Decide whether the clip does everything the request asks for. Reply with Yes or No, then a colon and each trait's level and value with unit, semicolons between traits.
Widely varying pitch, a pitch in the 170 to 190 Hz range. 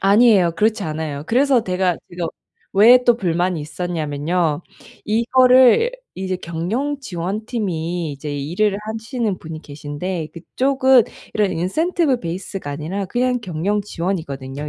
Yes: wide, 5.9 semitones; medium, 185 Hz